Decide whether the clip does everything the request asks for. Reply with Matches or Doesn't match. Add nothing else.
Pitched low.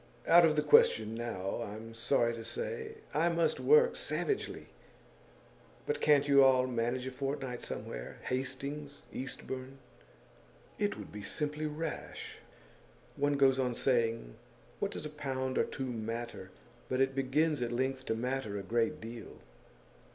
Matches